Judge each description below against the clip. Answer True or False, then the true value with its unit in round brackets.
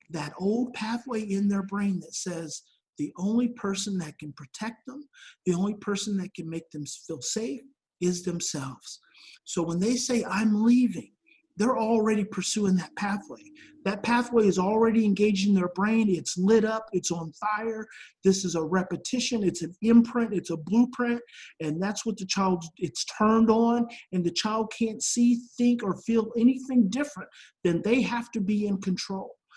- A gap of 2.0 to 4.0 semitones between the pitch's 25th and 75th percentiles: False (4.4 semitones)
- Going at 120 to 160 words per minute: False (175 wpm)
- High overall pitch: True (210 Hz)